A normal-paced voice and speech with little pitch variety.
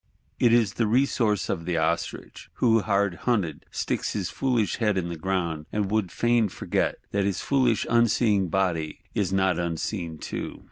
No: average, 170 wpm; average, 4.8 semitones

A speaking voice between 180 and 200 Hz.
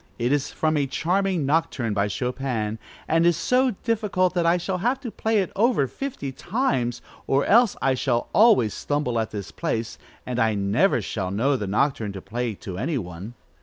No: low, 135 Hz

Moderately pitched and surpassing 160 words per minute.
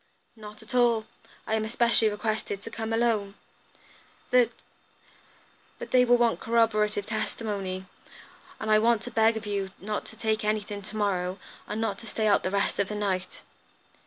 No: high, 215 Hz; average, 180 wpm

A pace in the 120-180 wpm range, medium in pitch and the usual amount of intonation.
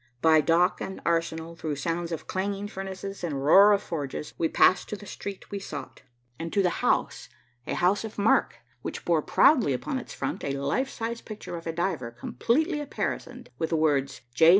No: average, 195 wpm; medium, 175 Hz; average, 4.2 semitones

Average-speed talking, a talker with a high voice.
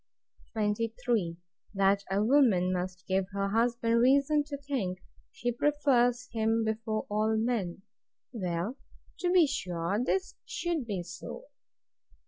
No: slow, 115 wpm; high, 225 Hz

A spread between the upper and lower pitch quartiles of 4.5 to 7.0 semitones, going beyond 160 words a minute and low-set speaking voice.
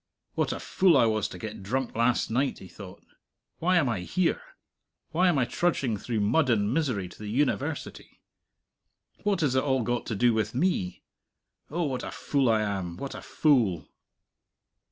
Yes: wide, 5.6 semitones; average, 180 wpm; low, 125 Hz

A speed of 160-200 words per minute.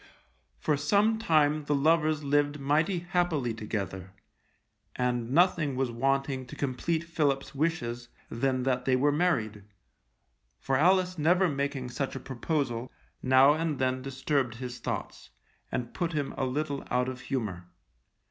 No: average, 140 wpm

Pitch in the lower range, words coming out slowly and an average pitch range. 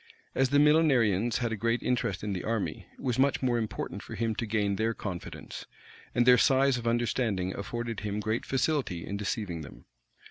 No: low, 115 Hz; average, 190 wpm; average, 3.5 semitones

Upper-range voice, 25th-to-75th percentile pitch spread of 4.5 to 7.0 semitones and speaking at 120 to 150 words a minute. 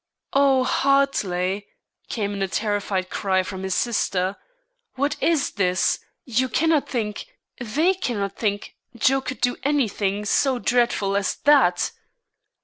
Yes: high, 220 Hz; wide, 5.5 semitones; slow, 135 wpm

